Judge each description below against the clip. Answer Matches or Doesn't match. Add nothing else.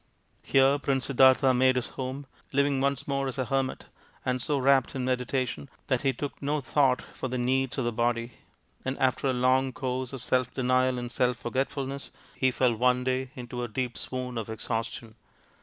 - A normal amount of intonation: Doesn't match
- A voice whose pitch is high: Doesn't match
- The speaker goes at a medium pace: Matches